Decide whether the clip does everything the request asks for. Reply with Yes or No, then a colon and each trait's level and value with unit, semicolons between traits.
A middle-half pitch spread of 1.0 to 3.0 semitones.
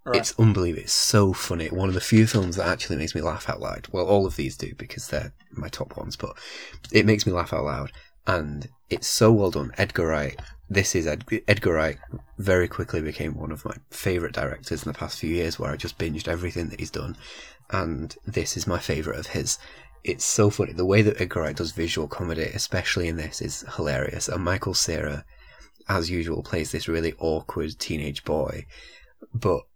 No: average, 3.8 semitones